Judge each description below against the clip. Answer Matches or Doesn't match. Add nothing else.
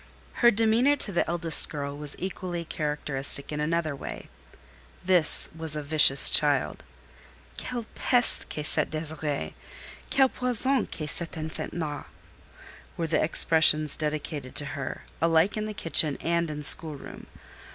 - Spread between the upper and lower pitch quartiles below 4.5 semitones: Matches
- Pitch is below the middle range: Doesn't match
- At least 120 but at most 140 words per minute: Matches